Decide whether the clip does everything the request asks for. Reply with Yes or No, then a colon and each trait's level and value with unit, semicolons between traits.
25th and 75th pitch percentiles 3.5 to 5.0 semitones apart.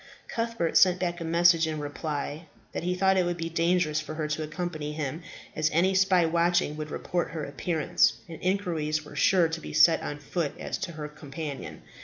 No: narrow, 2.4 semitones